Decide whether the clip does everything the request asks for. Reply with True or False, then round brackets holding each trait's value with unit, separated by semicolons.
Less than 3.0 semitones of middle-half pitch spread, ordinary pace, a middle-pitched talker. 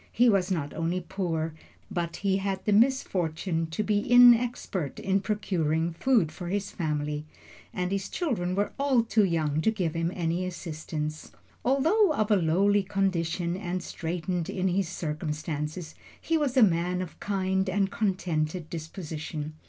False (3.8 semitones; 150 wpm; 180 Hz)